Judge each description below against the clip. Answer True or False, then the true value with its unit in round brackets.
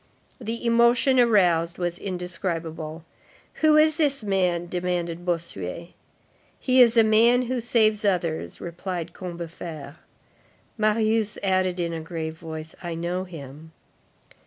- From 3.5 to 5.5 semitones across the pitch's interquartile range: True (4.8 semitones)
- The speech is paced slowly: True (120 wpm)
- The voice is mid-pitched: True (180 Hz)